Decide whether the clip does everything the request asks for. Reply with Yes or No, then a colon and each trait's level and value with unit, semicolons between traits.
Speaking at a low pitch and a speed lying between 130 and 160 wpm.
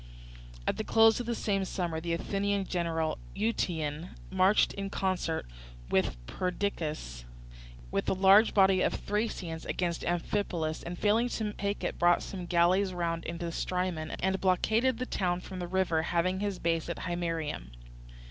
No: medium, 180 Hz; average, 155 wpm